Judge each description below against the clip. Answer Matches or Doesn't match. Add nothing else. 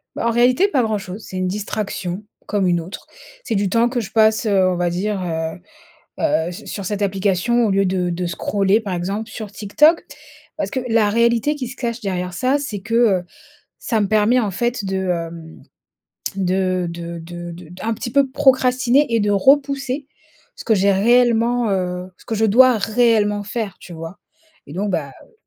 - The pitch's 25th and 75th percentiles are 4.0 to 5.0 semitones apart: Matches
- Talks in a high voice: Matches